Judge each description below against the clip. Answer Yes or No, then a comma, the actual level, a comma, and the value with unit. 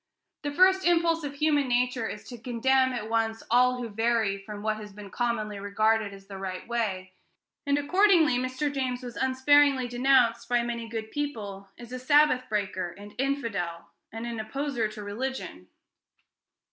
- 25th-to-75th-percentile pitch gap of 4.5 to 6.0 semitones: No, average, 4.1 semitones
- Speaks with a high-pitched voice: Yes, high, 240 Hz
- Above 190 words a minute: No, average, 165 wpm